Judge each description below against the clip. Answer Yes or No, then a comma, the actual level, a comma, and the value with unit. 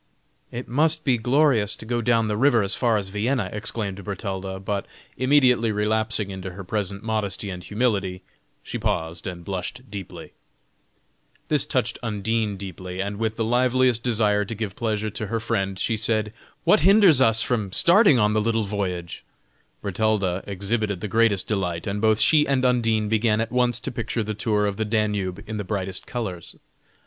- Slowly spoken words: No, average, 175 wpm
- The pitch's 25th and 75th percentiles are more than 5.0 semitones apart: No, average, 2.9 semitones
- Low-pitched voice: Yes, low, 110 Hz